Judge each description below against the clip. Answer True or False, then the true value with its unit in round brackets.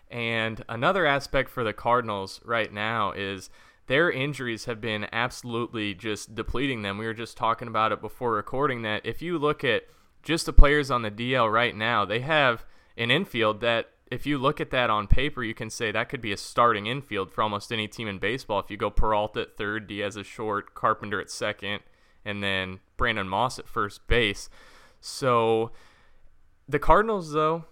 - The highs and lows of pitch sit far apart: False (3.5 semitones)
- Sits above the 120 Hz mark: False (115 Hz)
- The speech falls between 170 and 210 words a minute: True (190 wpm)